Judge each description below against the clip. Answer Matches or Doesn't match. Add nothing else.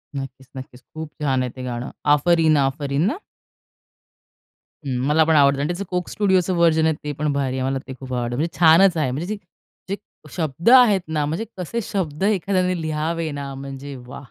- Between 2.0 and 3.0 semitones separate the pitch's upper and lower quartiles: Doesn't match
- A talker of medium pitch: Matches